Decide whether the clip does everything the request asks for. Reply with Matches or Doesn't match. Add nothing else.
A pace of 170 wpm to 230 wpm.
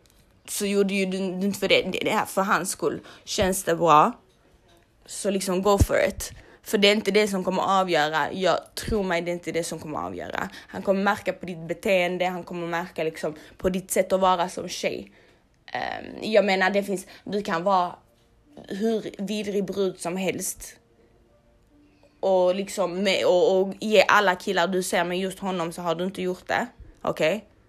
Matches